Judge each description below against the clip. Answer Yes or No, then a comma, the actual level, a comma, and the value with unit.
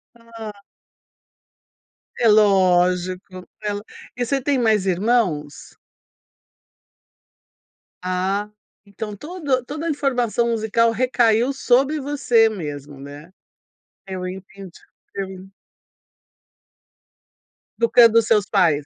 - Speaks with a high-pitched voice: Yes, high, 210 Hz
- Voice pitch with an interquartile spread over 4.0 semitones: Yes, average, 4.7 semitones